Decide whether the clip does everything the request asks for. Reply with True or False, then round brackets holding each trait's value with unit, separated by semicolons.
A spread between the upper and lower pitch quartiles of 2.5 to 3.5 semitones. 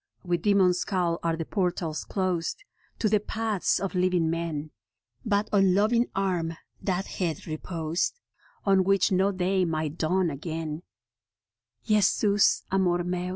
True (2.8 semitones)